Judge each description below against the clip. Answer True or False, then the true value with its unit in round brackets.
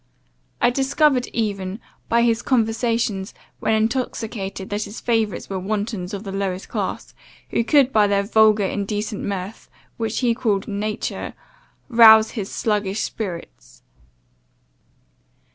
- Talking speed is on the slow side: True (125 wpm)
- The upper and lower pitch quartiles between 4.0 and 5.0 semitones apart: False (2.6 semitones)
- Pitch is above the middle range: True (215 Hz)